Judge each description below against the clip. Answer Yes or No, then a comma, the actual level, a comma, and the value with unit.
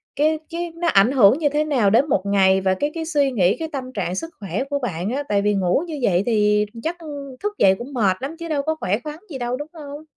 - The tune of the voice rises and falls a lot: Yes, wide, 7.2 semitones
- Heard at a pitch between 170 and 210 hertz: No, very high, 260 Hz